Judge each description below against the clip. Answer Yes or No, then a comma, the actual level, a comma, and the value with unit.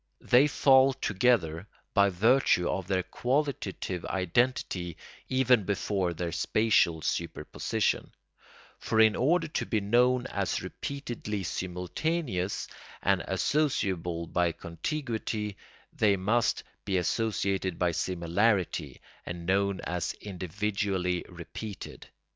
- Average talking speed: No, slow, 100 wpm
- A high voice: No, low, 100 Hz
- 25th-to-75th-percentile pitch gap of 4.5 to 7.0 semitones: Yes, average, 5.2 semitones